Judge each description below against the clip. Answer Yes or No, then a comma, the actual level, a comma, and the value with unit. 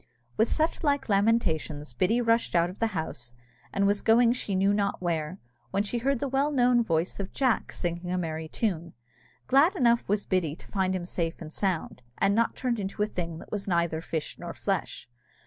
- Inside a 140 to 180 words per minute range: No, fast, 205 wpm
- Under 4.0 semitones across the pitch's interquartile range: No, wide, 5.4 semitones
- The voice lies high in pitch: Yes, high, 195 Hz